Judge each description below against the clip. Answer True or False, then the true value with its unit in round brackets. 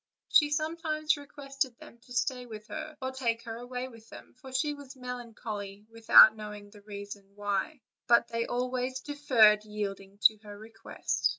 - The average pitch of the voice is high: True (235 Hz)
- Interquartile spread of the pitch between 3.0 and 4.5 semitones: True (3.8 semitones)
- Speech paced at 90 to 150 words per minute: False (160 wpm)